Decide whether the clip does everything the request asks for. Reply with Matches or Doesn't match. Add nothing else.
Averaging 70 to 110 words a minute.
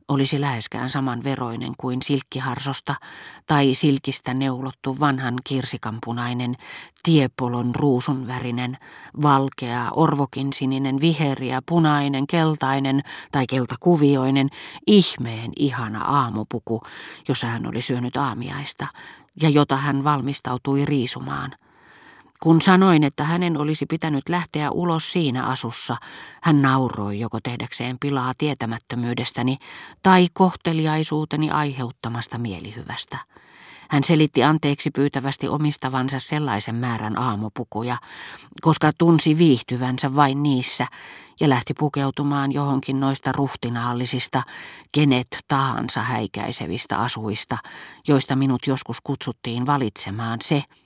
Matches